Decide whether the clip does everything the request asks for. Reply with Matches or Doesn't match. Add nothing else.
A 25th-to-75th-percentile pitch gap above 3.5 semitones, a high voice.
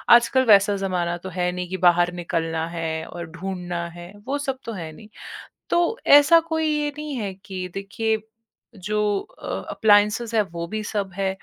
Matches